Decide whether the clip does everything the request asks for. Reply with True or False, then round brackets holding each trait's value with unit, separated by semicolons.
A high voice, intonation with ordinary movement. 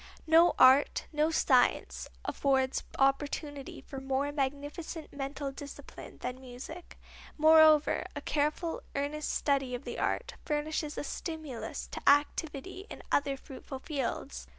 False (285 Hz; 2.3 semitones)